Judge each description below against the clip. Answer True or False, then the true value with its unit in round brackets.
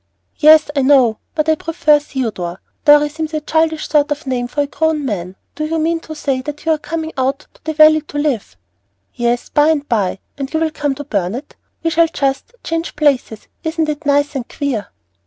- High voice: True (295 Hz)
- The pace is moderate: False (210 wpm)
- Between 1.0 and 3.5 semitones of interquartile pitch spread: True (3.0 semitones)